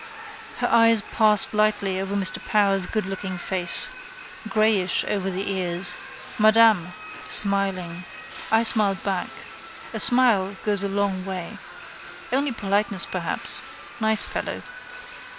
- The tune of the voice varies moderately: No, narrow, 2.3 semitones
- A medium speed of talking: No, slow, 115 wpm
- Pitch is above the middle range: Yes, high, 200 Hz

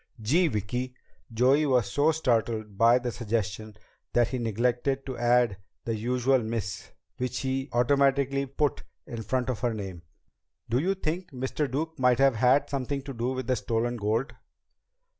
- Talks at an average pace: Yes, average, 160 wpm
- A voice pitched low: Yes, low, 125 Hz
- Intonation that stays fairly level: No, average, 3.0 semitones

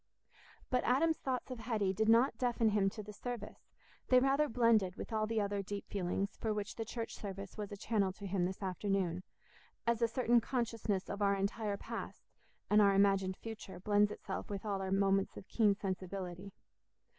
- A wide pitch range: No, average, 2.7 semitones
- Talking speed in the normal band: Yes, average, 190 wpm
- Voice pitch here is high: Yes, high, 205 Hz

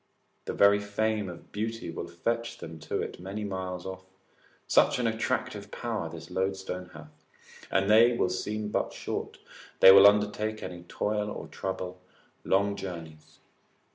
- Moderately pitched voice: No, low, 100 Hz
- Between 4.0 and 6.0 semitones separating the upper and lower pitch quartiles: No, average, 2.7 semitones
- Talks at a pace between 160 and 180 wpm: No, average, 150 wpm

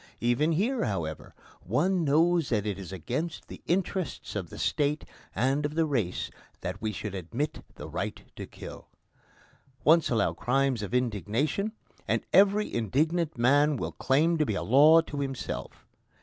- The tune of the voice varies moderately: No, wide, 6.6 semitones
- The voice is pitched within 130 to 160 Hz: Yes, medium, 140 Hz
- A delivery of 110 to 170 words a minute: Yes, average, 160 wpm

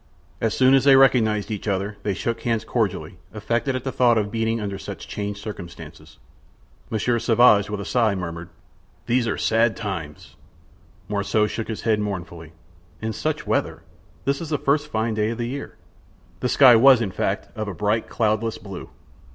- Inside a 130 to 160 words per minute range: No, average, 180 wpm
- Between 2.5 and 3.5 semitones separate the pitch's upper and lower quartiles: Yes, average, 2.8 semitones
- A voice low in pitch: Yes, low, 110 Hz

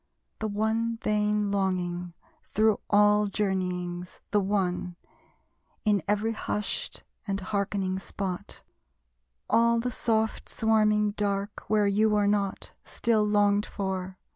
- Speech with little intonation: Yes, narrow, 1.8 semitones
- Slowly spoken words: Yes, slow, 115 wpm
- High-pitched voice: Yes, high, 205 Hz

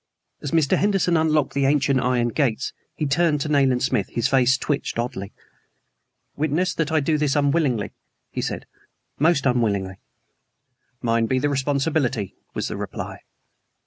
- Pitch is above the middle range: No, medium, 140 Hz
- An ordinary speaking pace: Yes, average, 145 wpm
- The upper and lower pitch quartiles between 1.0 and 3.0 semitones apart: No, average, 3.7 semitones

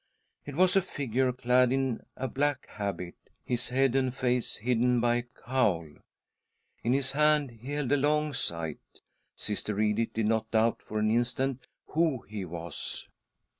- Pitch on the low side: Yes, low, 125 Hz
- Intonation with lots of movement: No, average, 3.7 semitones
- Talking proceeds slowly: No, average, 160 wpm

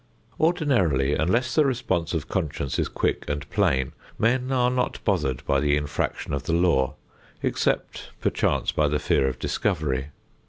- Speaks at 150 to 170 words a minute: Yes, average, 155 wpm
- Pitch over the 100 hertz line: No, very low, 80 Hz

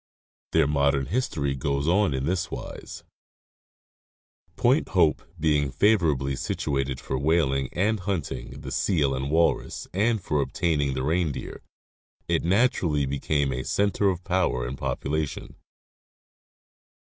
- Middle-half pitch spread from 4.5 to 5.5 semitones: Yes, average, 4.8 semitones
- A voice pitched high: No, very low, 75 Hz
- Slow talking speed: Yes, slow, 120 wpm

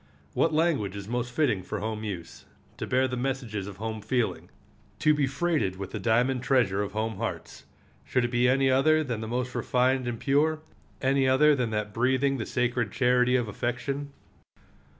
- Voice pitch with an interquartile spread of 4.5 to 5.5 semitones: No, average, 3.4 semitones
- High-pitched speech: No, low, 125 Hz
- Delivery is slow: No, average, 185 wpm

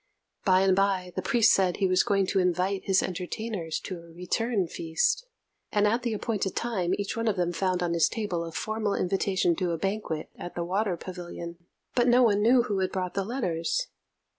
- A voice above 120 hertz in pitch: Yes, high, 190 Hz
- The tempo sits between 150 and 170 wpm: No, fast, 205 wpm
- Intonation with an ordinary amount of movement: Yes, average, 3.3 semitones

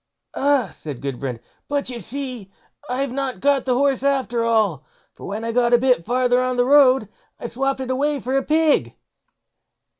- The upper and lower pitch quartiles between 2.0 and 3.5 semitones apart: Yes, average, 2.9 semitones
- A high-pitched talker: Yes, very high, 255 Hz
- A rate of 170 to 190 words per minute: Yes, average, 180 wpm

